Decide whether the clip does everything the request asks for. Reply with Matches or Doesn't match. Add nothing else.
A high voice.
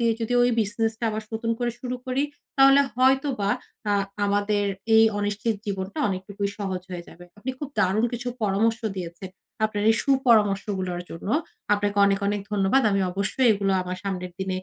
Matches